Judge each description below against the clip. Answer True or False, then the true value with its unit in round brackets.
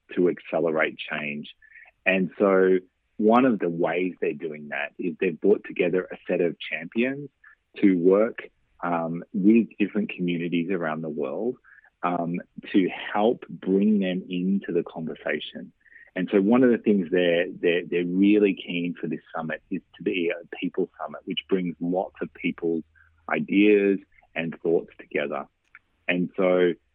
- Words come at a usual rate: True (150 wpm)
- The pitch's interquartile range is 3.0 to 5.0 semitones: False (2.5 semitones)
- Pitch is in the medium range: False (90 Hz)